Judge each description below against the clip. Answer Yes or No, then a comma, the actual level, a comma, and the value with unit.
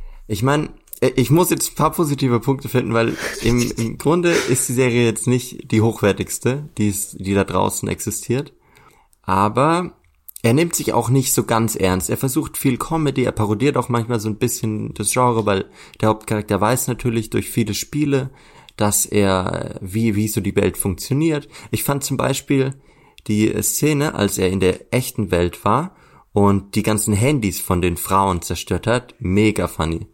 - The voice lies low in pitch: Yes, low, 115 Hz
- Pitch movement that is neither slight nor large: Yes, average, 4.7 semitones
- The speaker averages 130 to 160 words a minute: No, average, 175 wpm